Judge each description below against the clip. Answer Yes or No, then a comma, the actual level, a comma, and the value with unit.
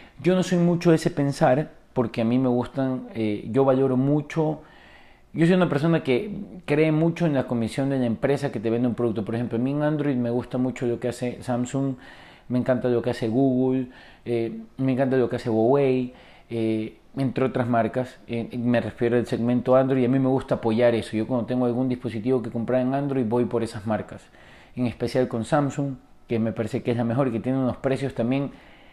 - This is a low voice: Yes, low, 125 Hz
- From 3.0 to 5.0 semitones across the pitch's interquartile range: No, narrow, 2.5 semitones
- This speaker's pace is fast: Yes, fast, 220 wpm